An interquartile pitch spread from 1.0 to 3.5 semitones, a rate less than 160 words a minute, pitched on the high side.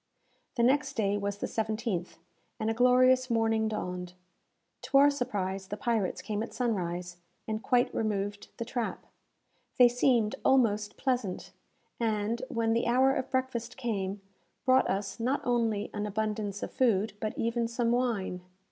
Yes: average, 3.2 semitones; average, 150 wpm; high, 225 Hz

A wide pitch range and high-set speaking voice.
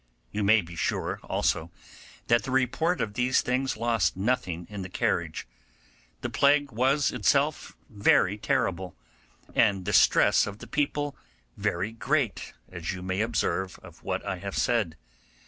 No: wide, 5.9 semitones; low, 110 Hz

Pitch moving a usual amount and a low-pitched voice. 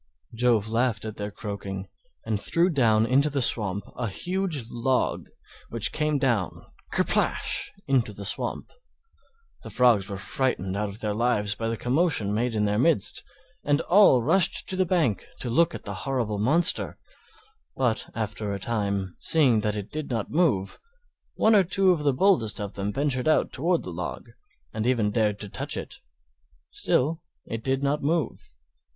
No: wide, 6.0 semitones; low, 120 Hz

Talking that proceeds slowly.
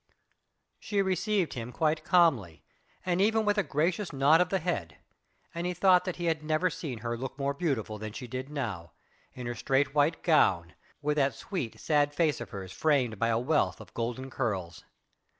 No: average, 190 wpm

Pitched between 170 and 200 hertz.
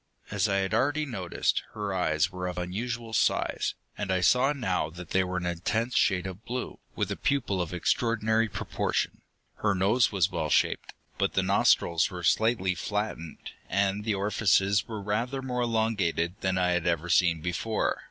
No: low, 100 Hz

